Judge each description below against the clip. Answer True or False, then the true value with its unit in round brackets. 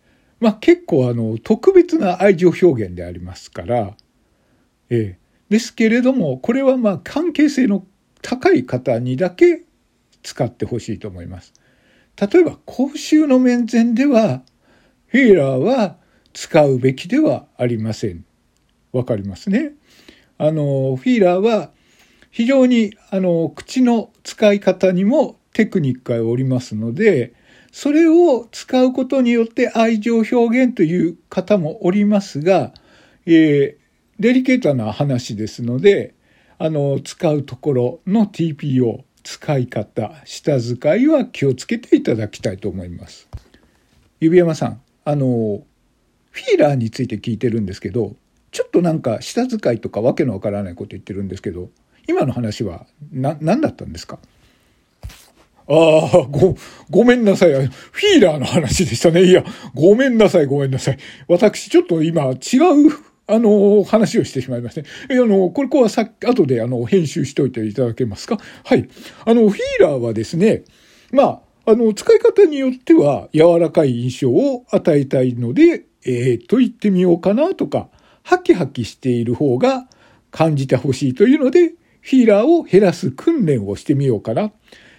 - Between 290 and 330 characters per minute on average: True (310 characters per minute)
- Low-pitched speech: False (175 Hz)